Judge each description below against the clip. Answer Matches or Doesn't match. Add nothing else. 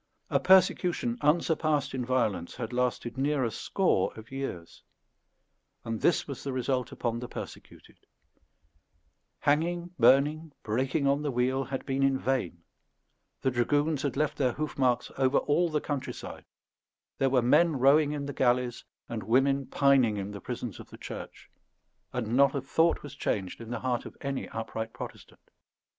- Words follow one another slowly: Doesn't match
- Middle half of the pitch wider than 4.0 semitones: Doesn't match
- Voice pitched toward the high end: Doesn't match